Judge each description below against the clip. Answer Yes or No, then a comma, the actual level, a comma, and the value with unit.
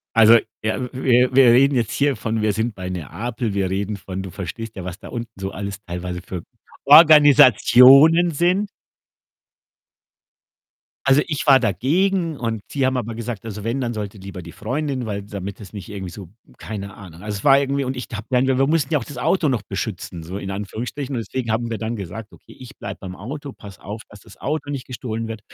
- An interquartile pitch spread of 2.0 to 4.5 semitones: No, average, 5.1 semitones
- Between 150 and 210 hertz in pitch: No, low, 115 Hz